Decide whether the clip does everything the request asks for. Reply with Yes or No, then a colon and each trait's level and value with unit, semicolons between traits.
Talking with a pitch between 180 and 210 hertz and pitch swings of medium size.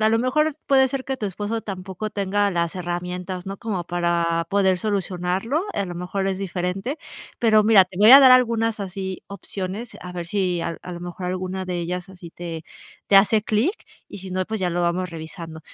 Yes: high, 190 Hz; average, 3.2 semitones